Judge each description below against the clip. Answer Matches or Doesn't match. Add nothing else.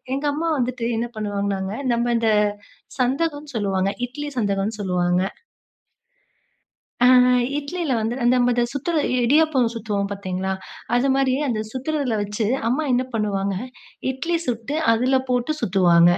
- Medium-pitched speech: Doesn't match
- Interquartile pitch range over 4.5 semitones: Matches